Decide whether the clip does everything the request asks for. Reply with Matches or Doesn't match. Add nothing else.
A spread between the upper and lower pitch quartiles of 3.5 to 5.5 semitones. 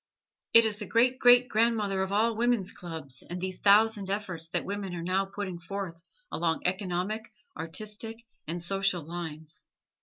Matches